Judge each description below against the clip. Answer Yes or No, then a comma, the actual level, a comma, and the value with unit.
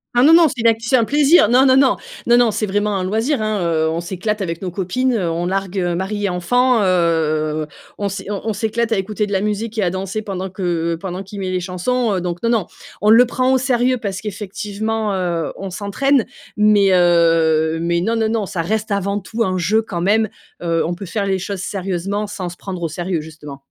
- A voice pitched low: No, high, 195 Hz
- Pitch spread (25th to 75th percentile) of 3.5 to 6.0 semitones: Yes, average, 3.9 semitones